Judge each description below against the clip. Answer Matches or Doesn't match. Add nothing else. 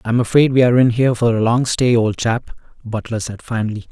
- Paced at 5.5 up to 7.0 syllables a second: Matches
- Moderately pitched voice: Doesn't match